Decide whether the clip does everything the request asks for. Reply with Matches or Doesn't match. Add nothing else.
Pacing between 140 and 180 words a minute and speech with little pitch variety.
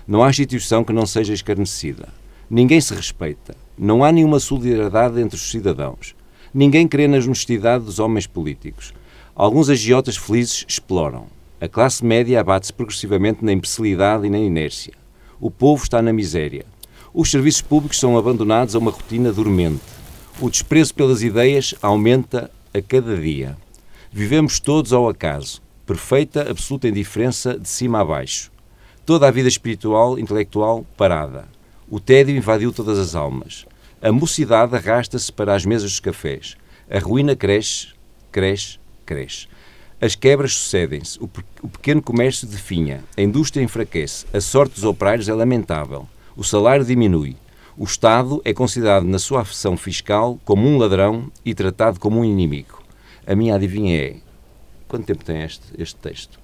Doesn't match